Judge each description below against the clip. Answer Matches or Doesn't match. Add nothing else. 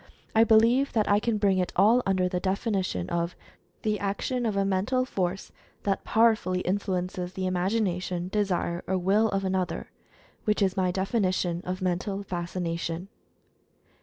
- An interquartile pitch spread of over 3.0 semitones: Doesn't match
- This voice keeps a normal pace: Matches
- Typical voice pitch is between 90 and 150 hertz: Doesn't match